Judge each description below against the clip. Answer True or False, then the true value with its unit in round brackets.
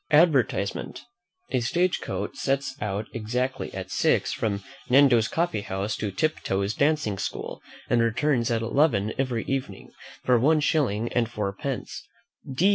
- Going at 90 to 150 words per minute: True (140 wpm)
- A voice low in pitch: True (120 Hz)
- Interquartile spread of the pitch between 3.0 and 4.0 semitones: False (4.7 semitones)